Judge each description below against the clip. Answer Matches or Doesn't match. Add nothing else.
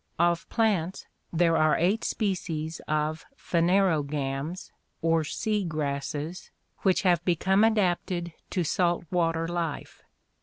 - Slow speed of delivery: Matches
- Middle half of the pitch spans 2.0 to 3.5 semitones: Matches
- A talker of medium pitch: Matches